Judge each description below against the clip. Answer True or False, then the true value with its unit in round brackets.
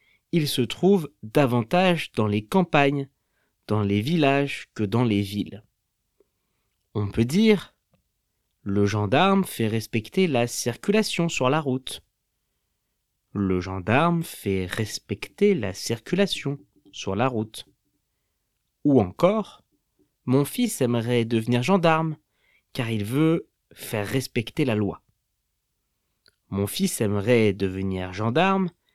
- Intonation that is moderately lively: False (7.5 semitones)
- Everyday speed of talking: False (110 wpm)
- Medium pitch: False (125 Hz)